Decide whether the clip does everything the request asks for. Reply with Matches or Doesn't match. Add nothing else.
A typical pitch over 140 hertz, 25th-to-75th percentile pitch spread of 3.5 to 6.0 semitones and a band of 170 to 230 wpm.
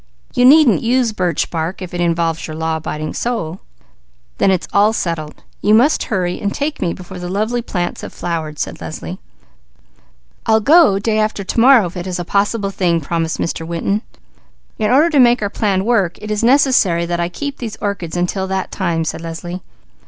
Matches